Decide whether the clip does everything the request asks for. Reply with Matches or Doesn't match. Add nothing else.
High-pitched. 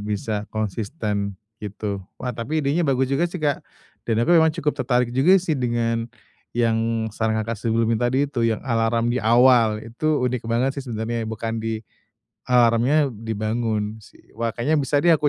Doesn't match